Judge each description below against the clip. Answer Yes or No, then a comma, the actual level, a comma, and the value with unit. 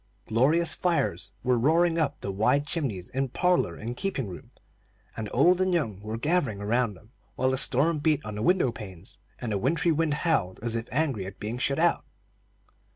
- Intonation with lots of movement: Yes, wide, 7.0 semitones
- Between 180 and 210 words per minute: Yes, average, 190 wpm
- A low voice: Yes, low, 130 Hz